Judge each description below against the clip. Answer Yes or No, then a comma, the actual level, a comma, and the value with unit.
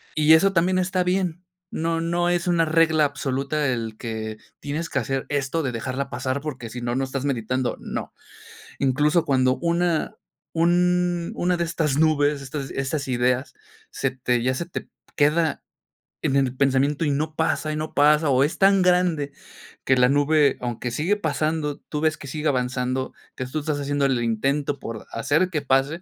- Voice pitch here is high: No, medium, 145 Hz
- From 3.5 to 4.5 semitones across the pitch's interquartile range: Yes, average, 3.8 semitones